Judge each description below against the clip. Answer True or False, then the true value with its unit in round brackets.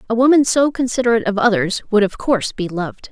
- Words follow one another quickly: True (210 wpm)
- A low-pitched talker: False (220 Hz)